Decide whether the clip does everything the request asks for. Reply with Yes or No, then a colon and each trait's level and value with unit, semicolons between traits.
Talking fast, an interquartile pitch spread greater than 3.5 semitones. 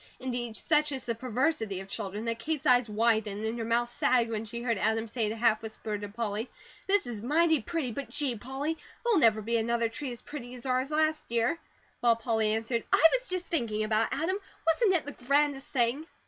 Yes: fast, 220 wpm; average, 4.7 semitones